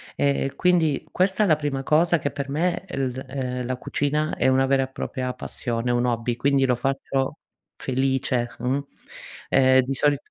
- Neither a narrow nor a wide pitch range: No, narrow, 2.3 semitones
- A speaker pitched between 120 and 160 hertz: Yes, low, 135 Hz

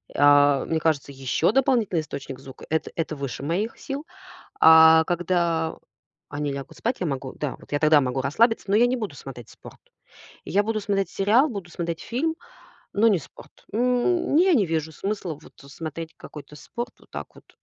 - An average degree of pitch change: No, wide, 7.1 semitones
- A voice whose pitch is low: No, medium, 165 Hz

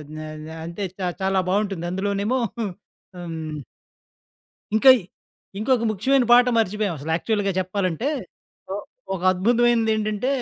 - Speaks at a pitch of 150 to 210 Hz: Yes, high, 205 Hz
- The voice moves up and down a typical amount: Yes, average, 3.8 semitones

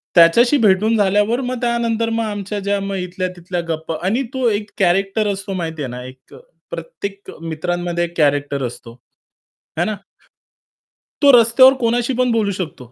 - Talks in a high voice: Yes, high, 195 Hz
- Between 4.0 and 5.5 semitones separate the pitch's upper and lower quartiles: Yes, average, 4.9 semitones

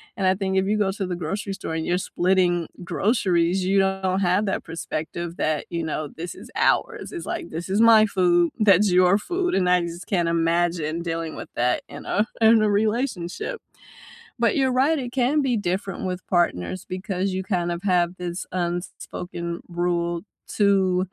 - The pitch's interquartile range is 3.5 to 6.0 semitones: No, average, 2.9 semitones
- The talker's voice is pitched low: No, medium, 185 Hz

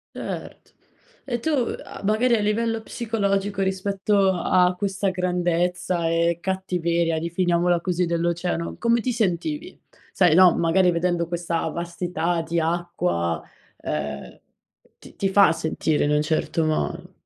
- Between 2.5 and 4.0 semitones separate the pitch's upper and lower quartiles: Yes, average, 2.8 semitones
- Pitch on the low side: No, medium, 180 Hz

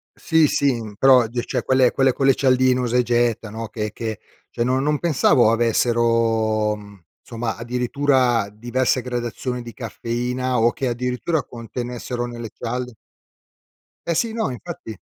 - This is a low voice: Yes, low, 120 Hz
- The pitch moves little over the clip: Yes, narrow, 1.9 semitones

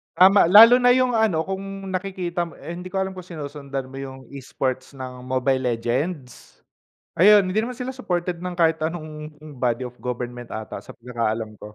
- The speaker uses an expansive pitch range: Yes, wide, 6.7 semitones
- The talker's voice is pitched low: No, medium, 160 Hz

